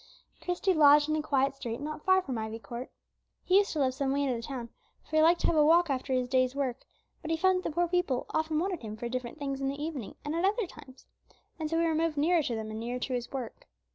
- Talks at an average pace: No, fast, 285 wpm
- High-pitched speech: Yes, very high, 285 Hz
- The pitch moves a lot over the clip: No, average, 4.4 semitones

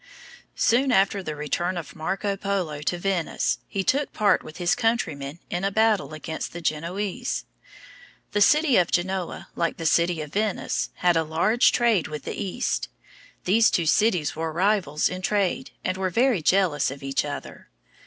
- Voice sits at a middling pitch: Yes, medium, 180 Hz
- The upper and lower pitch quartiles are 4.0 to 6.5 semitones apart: Yes, average, 4.5 semitones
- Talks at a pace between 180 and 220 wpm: No, average, 170 wpm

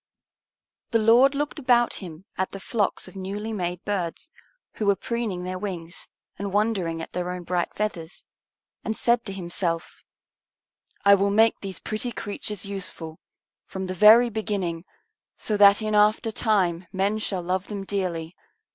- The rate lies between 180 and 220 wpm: No, average, 155 wpm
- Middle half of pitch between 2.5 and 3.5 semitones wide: Yes, average, 3.1 semitones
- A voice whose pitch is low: No, high, 200 Hz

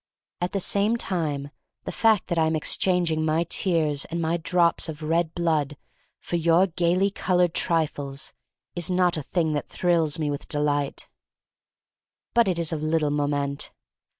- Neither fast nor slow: Yes, average, 155 wpm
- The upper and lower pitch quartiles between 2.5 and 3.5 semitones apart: Yes, average, 2.8 semitones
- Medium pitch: Yes, medium, 165 Hz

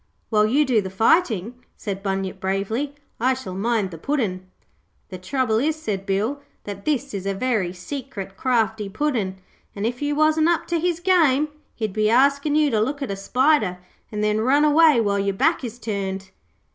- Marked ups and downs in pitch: Yes, wide, 6.3 semitones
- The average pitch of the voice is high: Yes, high, 225 Hz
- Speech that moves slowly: No, average, 185 wpm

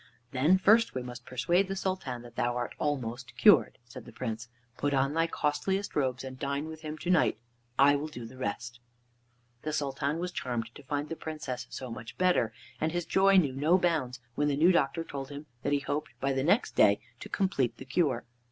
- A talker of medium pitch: Yes, medium, 145 Hz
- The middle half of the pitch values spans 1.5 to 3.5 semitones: No, average, 4.6 semitones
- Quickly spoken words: Yes, fast, 215 wpm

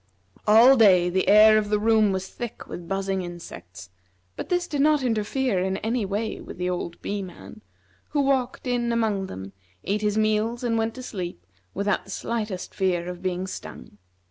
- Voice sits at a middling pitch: No, high, 205 Hz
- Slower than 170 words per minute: No, average, 185 wpm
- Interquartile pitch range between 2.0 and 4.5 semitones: Yes, average, 3.9 semitones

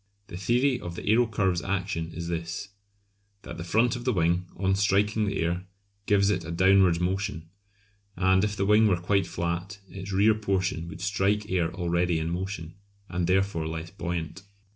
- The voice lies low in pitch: Yes, very low, 95 Hz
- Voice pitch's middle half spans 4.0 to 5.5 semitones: No, average, 2.8 semitones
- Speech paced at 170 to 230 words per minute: Yes, average, 175 wpm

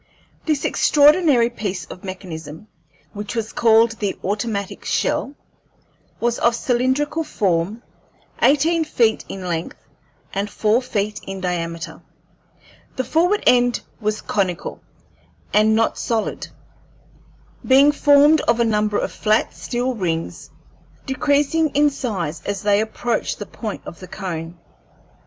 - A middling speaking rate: No, slow, 125 wpm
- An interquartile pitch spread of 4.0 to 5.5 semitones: Yes, average, 5.1 semitones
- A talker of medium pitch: No, high, 220 Hz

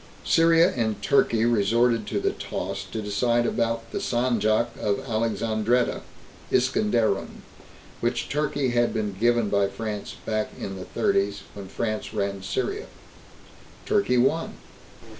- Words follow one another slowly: Yes, slow, 125 wpm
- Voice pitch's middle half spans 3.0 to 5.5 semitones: No, narrow, 2.6 semitones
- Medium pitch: No, low, 115 Hz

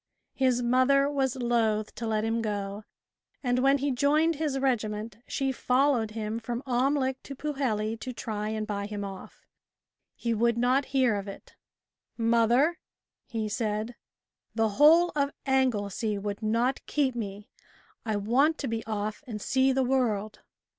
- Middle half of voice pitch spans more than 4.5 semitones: No, average, 3.8 semitones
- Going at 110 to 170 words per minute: Yes, average, 155 wpm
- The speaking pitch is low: No, high, 235 Hz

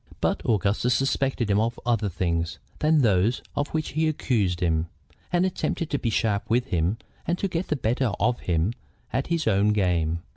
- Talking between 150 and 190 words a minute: Yes, average, 185 wpm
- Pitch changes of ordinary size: No, wide, 6.8 semitones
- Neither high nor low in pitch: No, low, 115 Hz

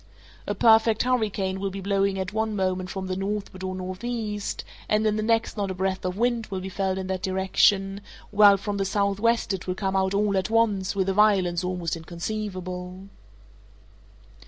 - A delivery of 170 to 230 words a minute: Yes, average, 185 wpm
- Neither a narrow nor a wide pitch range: No, narrow, 2.0 semitones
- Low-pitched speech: No, high, 195 Hz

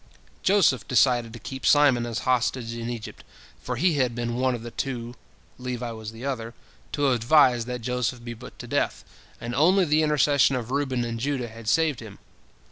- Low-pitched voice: Yes, low, 125 Hz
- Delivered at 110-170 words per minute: No, average, 180 wpm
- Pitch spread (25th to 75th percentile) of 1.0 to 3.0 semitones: Yes, average, 2.7 semitones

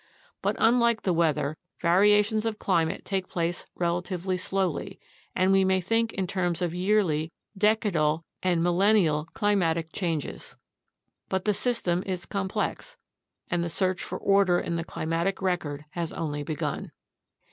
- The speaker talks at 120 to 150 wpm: Yes, average, 140 wpm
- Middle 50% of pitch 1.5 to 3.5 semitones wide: Yes, average, 3.0 semitones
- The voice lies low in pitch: No, medium, 180 Hz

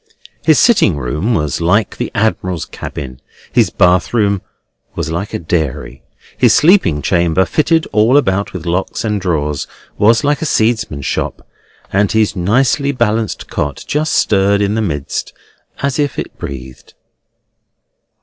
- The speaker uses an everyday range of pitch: No, wide, 5.9 semitones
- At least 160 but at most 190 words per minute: No, average, 145 wpm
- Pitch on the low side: Yes, low, 100 Hz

